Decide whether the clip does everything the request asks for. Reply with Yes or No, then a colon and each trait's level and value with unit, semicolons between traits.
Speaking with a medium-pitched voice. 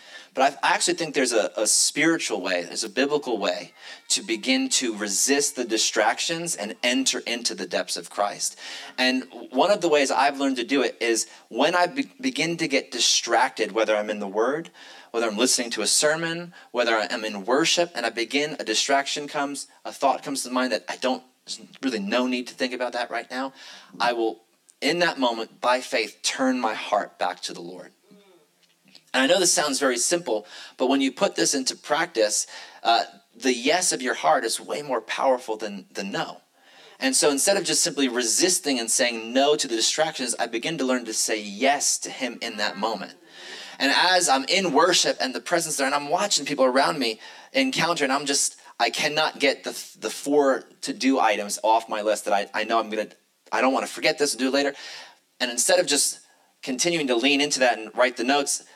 No: low, 120 Hz